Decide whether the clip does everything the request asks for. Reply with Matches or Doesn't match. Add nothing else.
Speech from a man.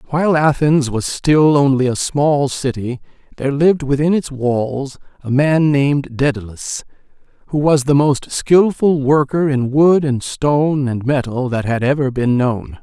Matches